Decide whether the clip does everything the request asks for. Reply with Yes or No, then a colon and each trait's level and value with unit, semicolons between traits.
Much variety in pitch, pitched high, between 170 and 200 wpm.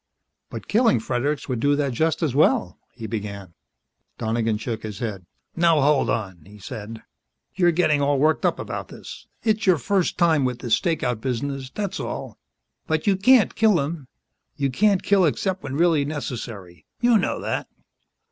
No: wide, 7.0 semitones; medium, 140 Hz; average, 175 wpm